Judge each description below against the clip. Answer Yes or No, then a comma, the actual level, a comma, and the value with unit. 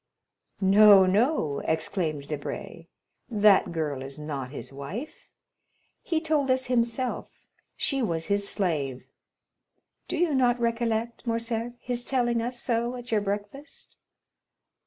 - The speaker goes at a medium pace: No, slow, 120 wpm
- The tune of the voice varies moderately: No, wide, 6.8 semitones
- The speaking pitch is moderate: No, high, 225 Hz